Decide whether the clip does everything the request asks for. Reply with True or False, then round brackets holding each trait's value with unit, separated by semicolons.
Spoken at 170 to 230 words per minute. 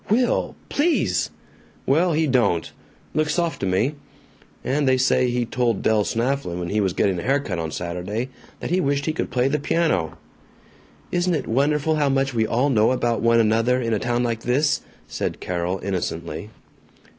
True (180 wpm)